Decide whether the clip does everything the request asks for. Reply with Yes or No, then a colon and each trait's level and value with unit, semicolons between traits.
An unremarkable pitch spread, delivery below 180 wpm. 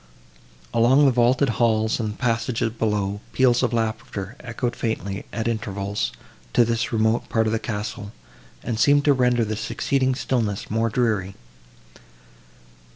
No: narrow, 2.2 semitones; average, 140 wpm